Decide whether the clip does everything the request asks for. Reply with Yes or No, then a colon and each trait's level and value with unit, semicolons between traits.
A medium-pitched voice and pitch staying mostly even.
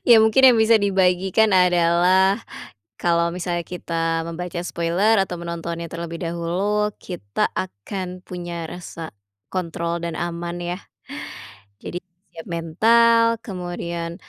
Yes: medium, 175 Hz; narrow, 2.0 semitones